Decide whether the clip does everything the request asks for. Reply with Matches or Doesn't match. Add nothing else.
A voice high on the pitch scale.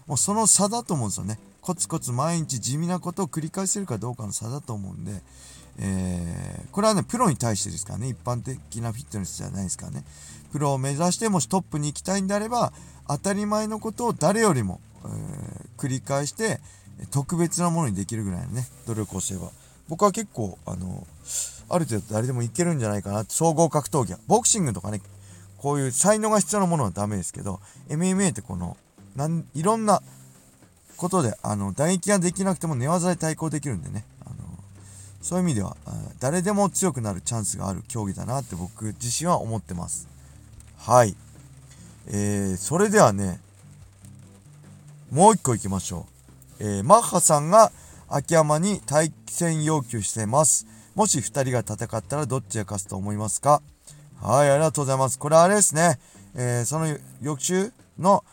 Doesn't match